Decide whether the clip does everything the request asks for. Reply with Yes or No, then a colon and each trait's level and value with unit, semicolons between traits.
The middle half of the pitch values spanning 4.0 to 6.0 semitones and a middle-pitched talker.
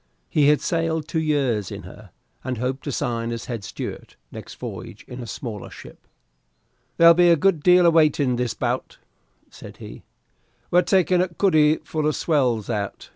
Yes: wide, 5.4 semitones; medium, 150 Hz